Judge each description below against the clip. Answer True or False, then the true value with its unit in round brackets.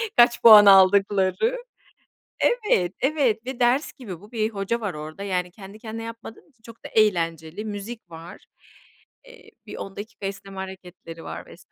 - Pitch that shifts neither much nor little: True (3.8 semitones)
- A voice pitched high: True (205 Hz)